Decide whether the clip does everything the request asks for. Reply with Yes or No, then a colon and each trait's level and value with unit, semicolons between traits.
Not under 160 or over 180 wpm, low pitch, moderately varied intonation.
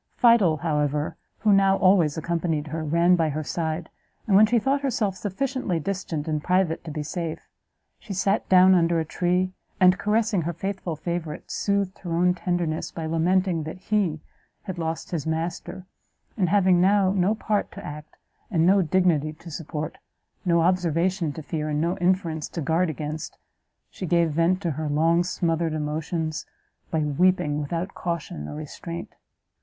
No: average, 165 wpm; medium, 170 Hz; average, 3.0 semitones